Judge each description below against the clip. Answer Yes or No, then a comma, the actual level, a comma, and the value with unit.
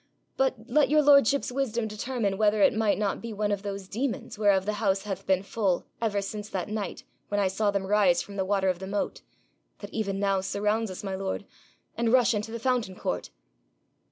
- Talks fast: Yes, fast, 210 wpm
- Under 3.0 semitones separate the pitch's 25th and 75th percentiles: Yes, narrow, 2.5 semitones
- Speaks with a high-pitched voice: Yes, high, 205 Hz